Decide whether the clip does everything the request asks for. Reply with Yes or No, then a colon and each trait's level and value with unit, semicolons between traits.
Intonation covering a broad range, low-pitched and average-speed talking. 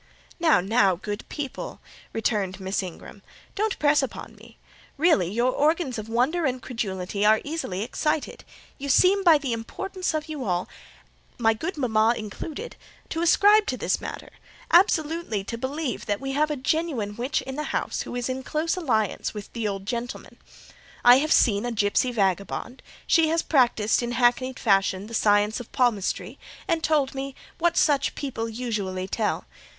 No: wide, 6.3 semitones; very high, 250 Hz; average, 160 wpm